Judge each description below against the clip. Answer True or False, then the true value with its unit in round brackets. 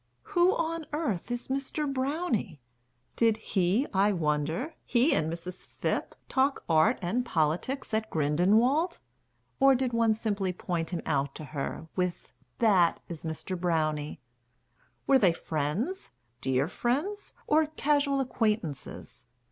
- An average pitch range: False (8.7 semitones)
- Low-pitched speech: False (215 Hz)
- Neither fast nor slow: False (130 wpm)